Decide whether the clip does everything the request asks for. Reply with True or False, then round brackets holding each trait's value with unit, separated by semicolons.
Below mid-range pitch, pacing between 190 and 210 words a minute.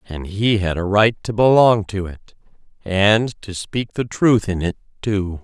False (100 Hz; 175 wpm)